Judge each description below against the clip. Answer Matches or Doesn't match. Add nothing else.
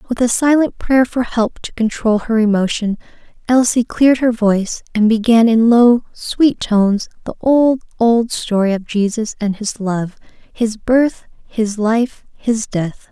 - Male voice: Doesn't match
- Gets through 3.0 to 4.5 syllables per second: Matches